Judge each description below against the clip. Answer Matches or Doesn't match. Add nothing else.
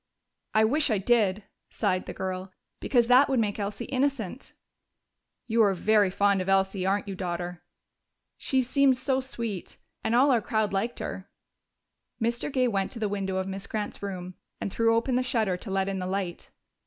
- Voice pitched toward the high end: Matches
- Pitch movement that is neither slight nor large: Matches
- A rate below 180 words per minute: Doesn't match